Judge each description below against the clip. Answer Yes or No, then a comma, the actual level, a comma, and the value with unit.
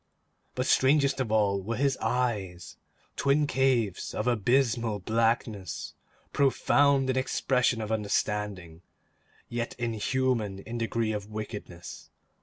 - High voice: No, low, 115 Hz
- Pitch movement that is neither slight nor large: Yes, average, 3.8 semitones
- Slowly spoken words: Yes, slow, 110 wpm